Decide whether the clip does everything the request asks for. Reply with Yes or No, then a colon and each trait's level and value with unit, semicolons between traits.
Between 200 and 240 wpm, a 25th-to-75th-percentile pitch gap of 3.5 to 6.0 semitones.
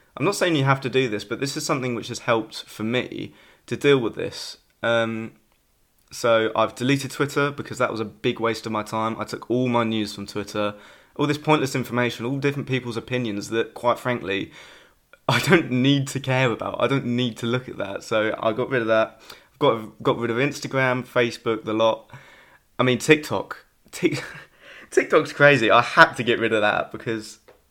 No: fast, 205 wpm; average, 3.0 semitones